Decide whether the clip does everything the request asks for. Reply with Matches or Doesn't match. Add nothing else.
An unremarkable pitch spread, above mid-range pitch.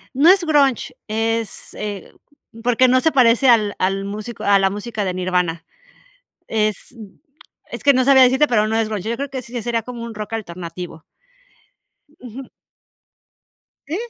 Matches